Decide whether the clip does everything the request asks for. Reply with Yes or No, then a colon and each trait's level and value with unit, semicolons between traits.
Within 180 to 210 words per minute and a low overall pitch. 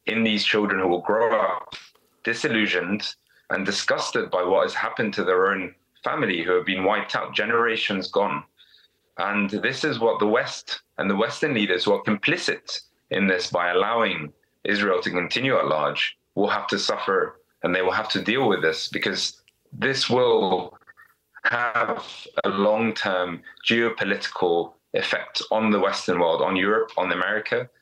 No: average, 165 wpm; low, 115 Hz